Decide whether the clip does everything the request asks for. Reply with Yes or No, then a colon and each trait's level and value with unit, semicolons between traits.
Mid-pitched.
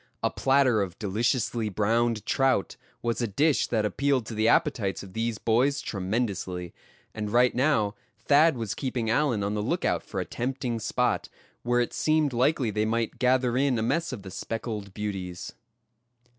No: low, 115 Hz